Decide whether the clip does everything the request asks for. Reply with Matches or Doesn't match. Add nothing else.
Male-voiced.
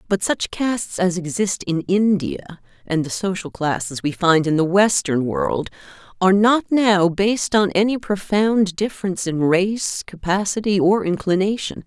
Doesn't match